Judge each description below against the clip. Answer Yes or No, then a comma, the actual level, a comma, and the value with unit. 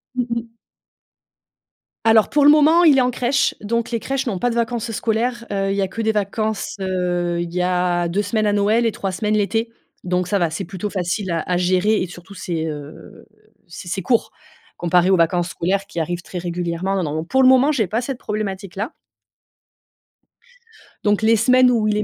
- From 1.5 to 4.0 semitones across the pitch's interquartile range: No, average, 4.4 semitones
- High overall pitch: Yes, high, 200 Hz